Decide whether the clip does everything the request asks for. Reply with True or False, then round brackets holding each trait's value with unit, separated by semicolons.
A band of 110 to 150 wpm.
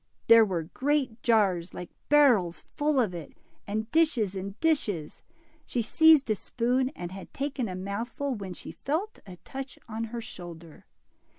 False (160 wpm)